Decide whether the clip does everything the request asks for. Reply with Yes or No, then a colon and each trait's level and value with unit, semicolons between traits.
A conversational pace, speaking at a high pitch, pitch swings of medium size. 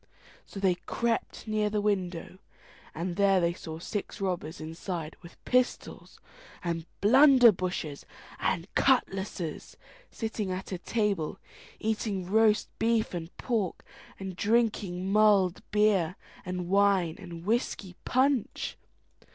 No: slow, 115 wpm; high, 195 Hz; average, 3.4 semitones